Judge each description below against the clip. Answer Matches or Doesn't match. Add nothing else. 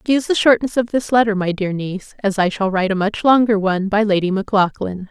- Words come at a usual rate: Doesn't match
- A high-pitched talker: Matches